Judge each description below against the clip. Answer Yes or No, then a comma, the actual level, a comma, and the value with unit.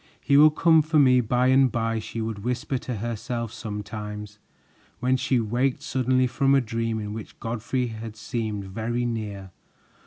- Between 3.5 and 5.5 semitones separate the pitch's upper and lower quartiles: No, average, 2.8 semitones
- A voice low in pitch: Yes, low, 115 Hz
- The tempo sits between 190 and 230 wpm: No, average, 165 wpm